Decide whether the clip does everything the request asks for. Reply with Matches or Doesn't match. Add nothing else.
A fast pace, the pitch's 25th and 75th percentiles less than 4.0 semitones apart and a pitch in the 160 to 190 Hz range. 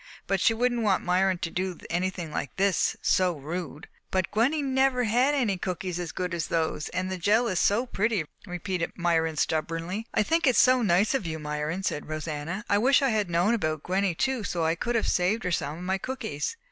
Doesn't match